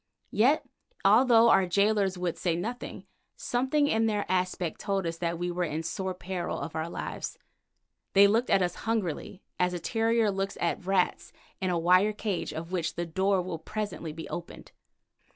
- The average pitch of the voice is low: No, medium, 185 Hz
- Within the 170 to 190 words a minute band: Yes, average, 175 wpm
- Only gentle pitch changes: No, average, 3.7 semitones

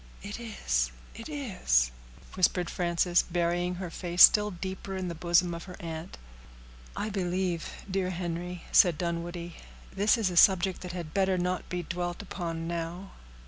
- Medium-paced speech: Yes, average, 150 wpm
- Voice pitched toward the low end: No, medium, 175 Hz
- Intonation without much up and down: Yes, narrow, 1.7 semitones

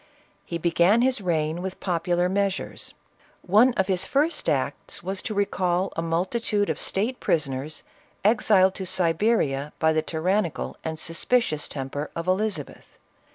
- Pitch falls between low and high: Yes, medium, 180 Hz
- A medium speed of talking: Yes, average, 145 wpm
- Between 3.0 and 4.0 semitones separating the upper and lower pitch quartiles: Yes, average, 3.7 semitones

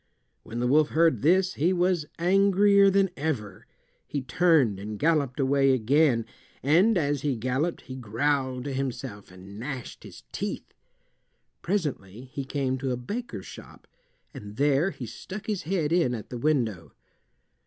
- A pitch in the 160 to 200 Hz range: No, medium, 140 Hz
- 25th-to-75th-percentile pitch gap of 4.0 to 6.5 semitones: Yes, wide, 5.5 semitones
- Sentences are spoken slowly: No, average, 155 wpm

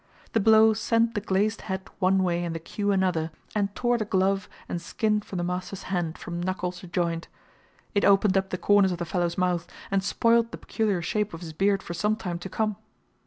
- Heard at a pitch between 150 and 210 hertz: Yes, high, 190 Hz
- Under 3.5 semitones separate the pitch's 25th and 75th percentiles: Yes, average, 3.1 semitones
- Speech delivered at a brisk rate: Yes, fast, 215 wpm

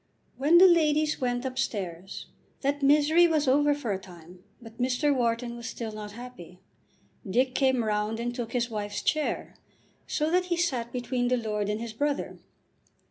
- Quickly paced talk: No, average, 170 wpm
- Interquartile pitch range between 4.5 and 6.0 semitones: Yes, average, 4.8 semitones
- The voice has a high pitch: Yes, high, 245 Hz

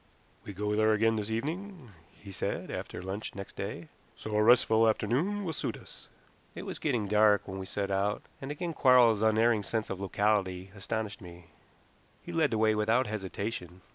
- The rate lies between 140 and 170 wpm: No, average, 180 wpm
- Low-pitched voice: Yes, low, 110 Hz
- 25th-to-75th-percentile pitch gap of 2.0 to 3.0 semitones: Yes, average, 2.7 semitones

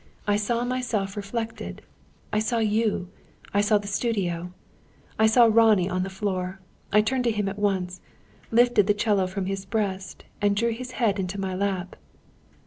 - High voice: Yes, high, 205 Hz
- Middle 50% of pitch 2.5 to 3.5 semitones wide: Yes, average, 2.8 semitones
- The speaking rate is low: No, average, 170 wpm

